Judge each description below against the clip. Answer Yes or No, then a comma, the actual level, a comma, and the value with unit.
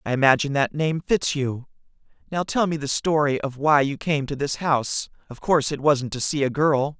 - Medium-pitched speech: Yes, medium, 145 Hz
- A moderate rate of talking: No, fast, 225 wpm